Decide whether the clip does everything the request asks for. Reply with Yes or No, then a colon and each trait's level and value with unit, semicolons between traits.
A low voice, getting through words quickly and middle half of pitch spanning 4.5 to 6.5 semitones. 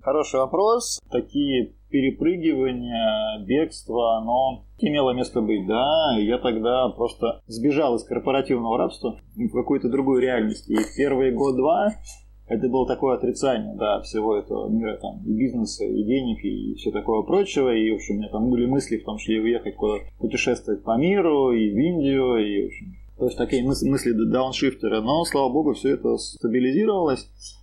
Yes: low, 130 Hz; fast, 165 wpm; average, 5.3 semitones